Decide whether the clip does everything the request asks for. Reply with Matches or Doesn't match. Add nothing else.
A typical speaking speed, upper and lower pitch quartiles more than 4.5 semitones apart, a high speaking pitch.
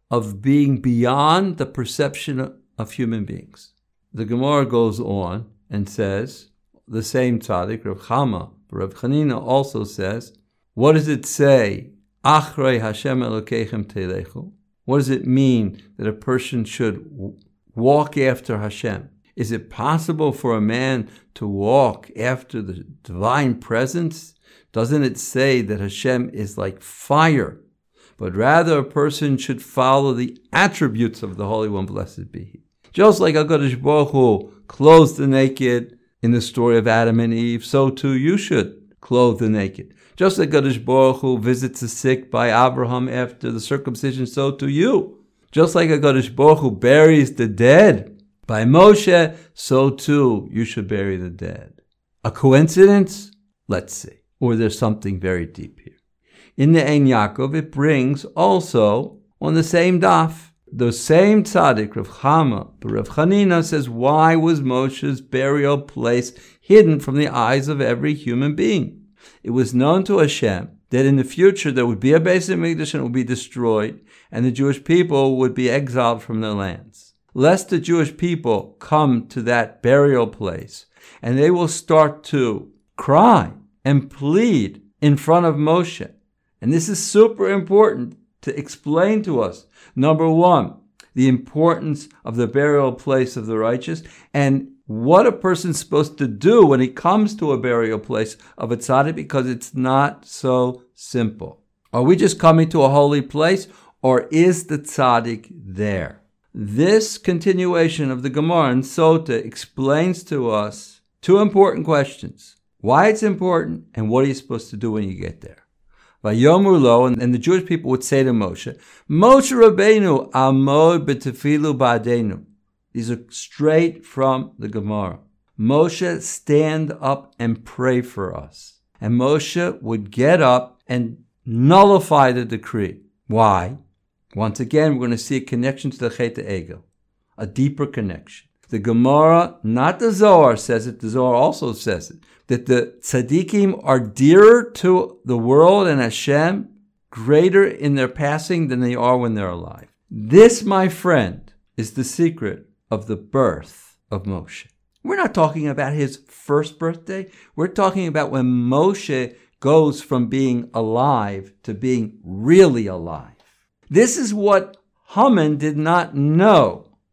Doesn't match